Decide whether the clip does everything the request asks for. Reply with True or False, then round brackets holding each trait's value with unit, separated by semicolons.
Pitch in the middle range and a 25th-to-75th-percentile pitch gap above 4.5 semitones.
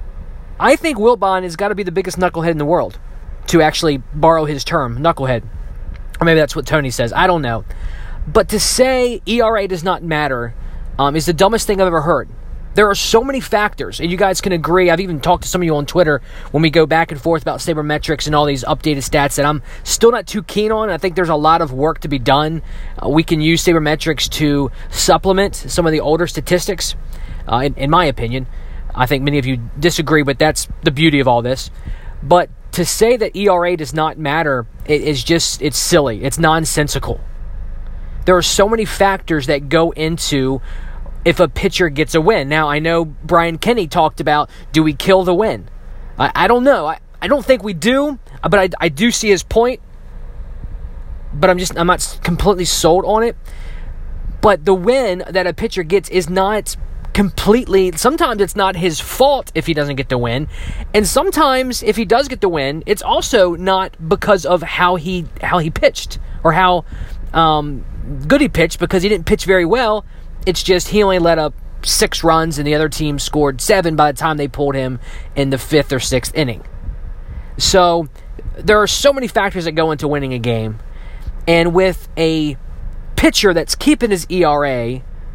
True (160 Hz; 5.2 semitones)